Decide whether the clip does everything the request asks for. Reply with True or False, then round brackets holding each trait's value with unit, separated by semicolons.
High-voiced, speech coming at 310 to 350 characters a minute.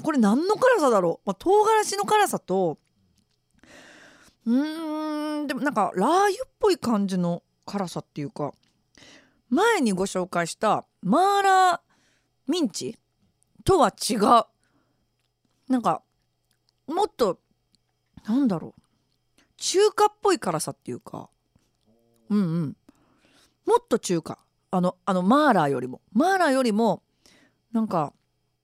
False (245 Hz; 235 characters per minute)